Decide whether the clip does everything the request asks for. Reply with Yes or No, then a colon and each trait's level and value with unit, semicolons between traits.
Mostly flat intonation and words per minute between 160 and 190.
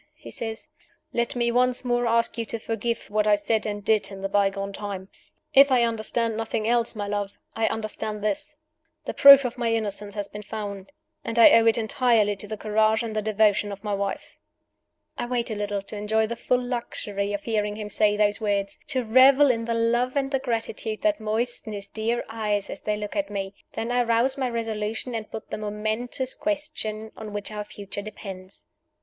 No: narrow, 2.3 semitones; fast, 205 wpm